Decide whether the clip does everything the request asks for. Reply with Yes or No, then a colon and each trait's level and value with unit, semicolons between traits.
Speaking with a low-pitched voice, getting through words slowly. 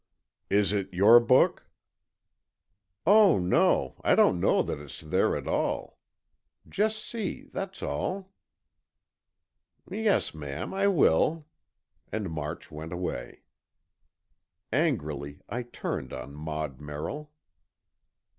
Yes: very low, 95 Hz; slow, 105 wpm